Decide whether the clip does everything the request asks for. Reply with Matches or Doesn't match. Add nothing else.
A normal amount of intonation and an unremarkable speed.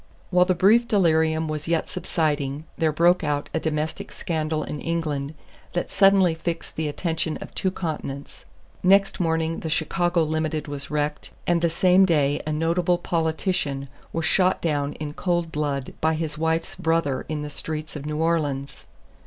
Doesn't match